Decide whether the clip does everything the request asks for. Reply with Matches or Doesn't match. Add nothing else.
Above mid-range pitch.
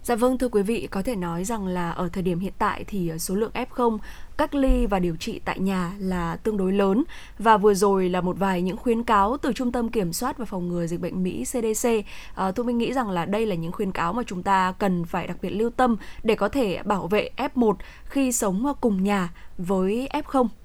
Matches